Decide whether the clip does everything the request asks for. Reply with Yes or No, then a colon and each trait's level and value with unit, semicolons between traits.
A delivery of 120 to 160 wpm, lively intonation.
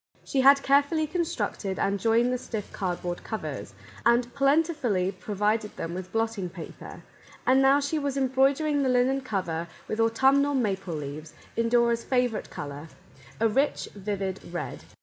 Yes: average, 150 wpm; wide, 5.9 semitones